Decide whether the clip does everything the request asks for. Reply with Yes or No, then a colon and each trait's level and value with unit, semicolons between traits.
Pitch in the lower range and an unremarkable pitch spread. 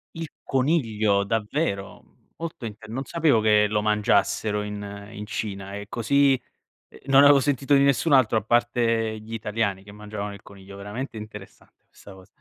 Yes: low, 110 Hz; average, 4.2 semitones